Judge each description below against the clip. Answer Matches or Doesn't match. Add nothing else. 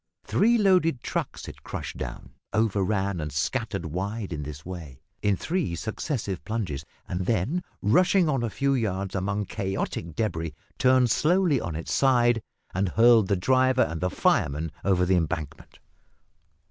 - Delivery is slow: Doesn't match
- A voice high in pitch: Doesn't match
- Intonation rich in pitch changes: Matches